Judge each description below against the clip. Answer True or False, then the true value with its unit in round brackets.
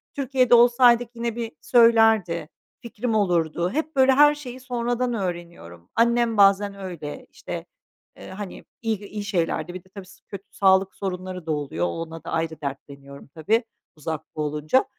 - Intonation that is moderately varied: False (6.3 semitones)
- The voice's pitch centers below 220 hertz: True (195 Hz)